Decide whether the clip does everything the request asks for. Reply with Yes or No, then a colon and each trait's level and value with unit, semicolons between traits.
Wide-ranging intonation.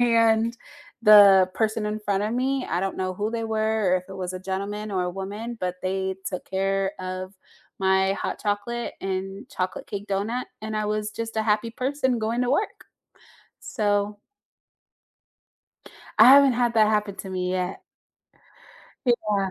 No: average, 2.8 semitones